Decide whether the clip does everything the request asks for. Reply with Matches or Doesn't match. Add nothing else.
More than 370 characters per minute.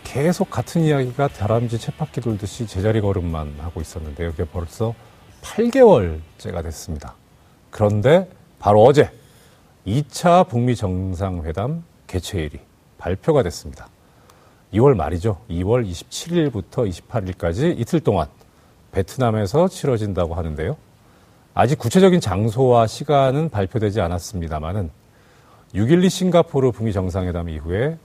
Doesn't match